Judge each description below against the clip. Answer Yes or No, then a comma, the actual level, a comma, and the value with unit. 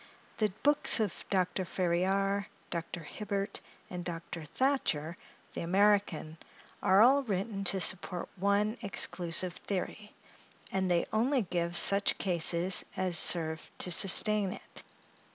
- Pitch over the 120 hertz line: Yes, high, 190 Hz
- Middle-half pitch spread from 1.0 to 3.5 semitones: Yes, average, 2.9 semitones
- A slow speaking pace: Yes, slow, 120 wpm